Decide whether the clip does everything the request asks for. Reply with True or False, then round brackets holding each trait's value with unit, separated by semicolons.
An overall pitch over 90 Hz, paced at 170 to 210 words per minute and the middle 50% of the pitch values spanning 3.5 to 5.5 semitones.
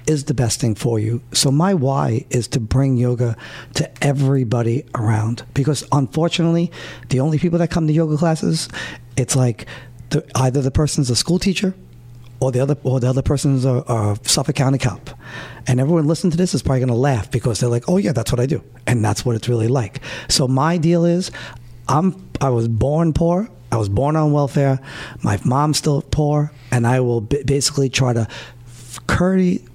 True (135 Hz; 200 wpm; 3.9 semitones)